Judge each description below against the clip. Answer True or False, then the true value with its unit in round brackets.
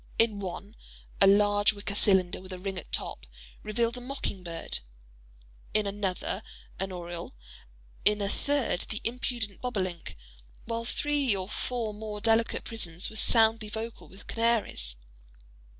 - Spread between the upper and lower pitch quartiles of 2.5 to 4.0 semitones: True (3.6 semitones)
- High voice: True (205 Hz)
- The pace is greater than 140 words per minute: False (135 wpm)